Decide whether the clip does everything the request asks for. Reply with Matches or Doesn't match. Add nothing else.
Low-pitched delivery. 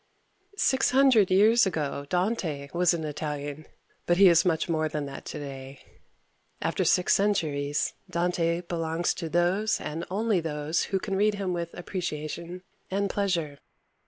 Doesn't match